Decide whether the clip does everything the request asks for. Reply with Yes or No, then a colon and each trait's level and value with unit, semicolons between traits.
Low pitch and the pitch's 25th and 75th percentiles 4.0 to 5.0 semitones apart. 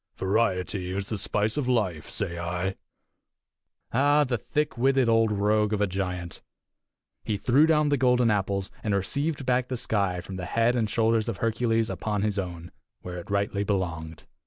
Yes: low, 105 Hz; average, 4.3 semitones